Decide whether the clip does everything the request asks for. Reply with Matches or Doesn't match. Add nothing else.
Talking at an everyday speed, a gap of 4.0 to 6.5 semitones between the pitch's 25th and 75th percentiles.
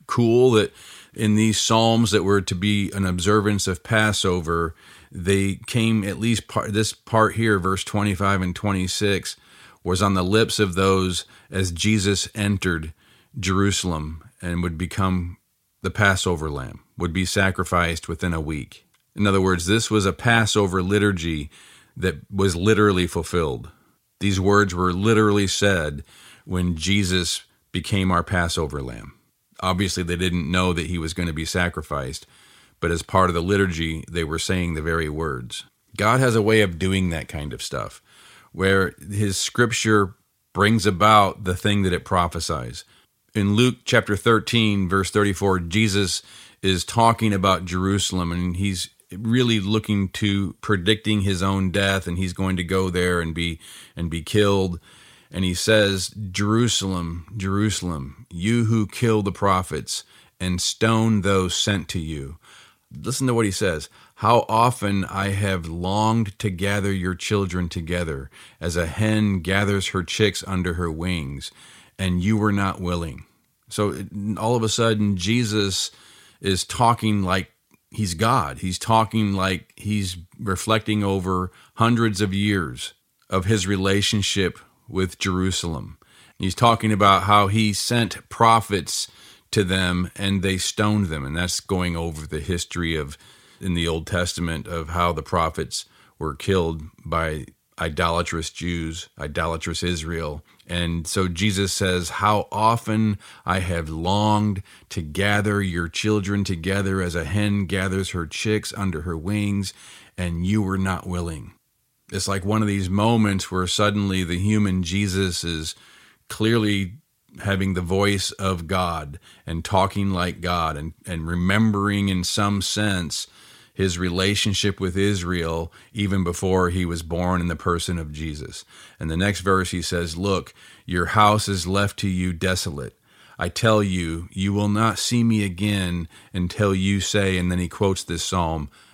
Doesn't match